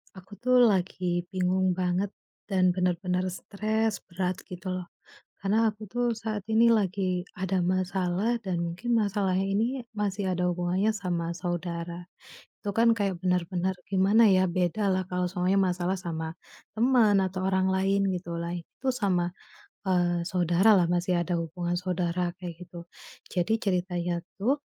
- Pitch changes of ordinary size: No, narrow, 2.2 semitones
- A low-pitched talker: No, medium, 185 Hz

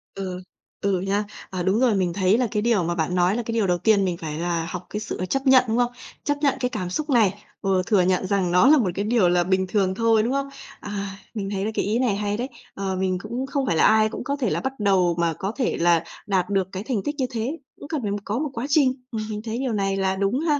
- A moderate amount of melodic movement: Yes, average, 4.4 semitones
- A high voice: Yes, high, 205 Hz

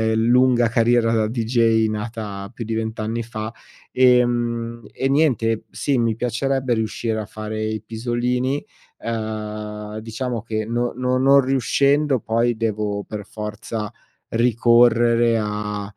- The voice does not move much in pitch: Yes, narrow, 2.0 semitones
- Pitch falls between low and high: No, low, 115 Hz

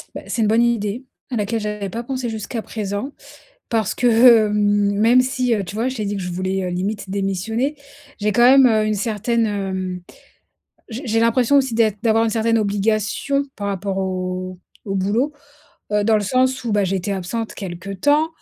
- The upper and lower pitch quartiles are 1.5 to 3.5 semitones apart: Yes, average, 3.0 semitones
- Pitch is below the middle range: No, high, 215 Hz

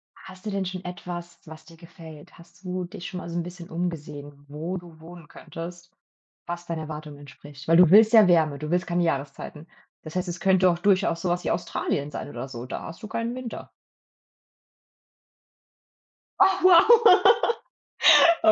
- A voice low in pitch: No, medium, 170 Hz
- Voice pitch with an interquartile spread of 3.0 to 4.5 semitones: No, narrow, 2.6 semitones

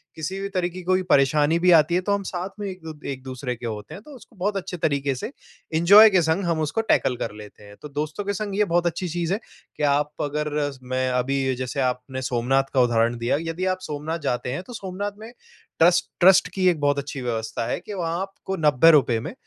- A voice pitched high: No, medium, 160 Hz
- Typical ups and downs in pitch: No, wide, 5.9 semitones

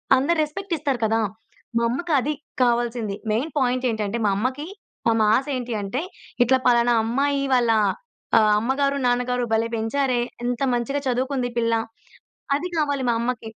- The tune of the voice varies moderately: Yes, average, 3.2 semitones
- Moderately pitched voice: No, high, 245 Hz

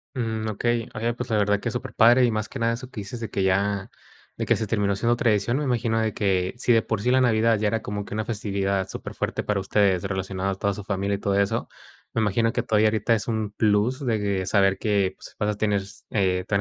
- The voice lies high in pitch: No, low, 105 Hz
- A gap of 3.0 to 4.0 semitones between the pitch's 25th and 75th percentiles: No, narrow, 2.6 semitones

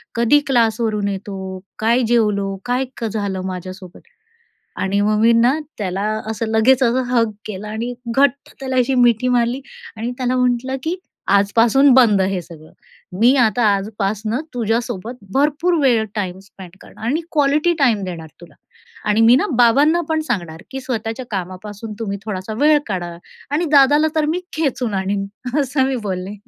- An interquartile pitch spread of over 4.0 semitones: Yes, average, 4.5 semitones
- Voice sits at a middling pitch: No, high, 225 Hz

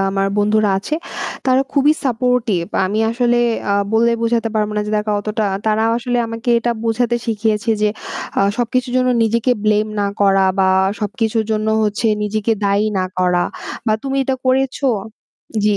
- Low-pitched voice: No, high, 225 Hz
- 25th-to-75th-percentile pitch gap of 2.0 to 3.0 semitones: Yes, narrow, 2.5 semitones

